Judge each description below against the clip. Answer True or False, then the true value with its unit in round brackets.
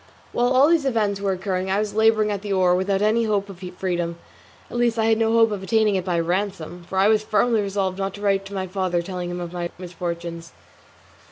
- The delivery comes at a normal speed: False (235 wpm)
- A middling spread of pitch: True (3.1 semitones)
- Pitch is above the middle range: True (195 Hz)